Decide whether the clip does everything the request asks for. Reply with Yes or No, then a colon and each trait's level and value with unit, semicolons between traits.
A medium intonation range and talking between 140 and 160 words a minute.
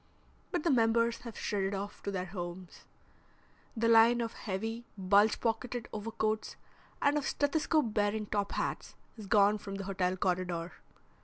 Yes: average, 3.1 semitones; average, 150 wpm